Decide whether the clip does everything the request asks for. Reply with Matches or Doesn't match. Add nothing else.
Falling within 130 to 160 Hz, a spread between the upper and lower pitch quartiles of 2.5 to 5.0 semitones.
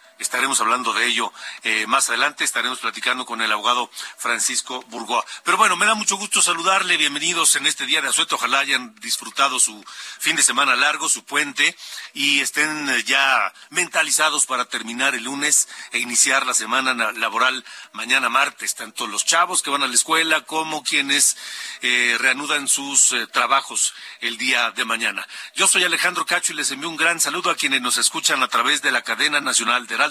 Matches